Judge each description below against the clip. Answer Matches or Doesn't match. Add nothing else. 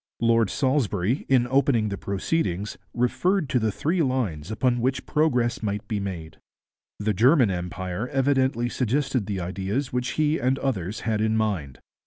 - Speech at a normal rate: Matches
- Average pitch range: Matches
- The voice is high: Doesn't match